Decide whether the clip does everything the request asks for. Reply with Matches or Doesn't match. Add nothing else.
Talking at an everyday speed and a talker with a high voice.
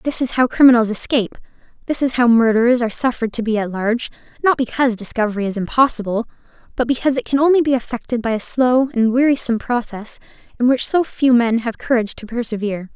Matches